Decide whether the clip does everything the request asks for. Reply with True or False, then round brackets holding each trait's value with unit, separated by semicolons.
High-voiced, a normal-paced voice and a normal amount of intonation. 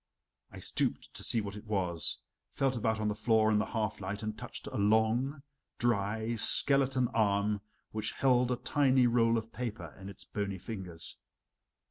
False (110 Hz; 170 wpm; 3.0 semitones)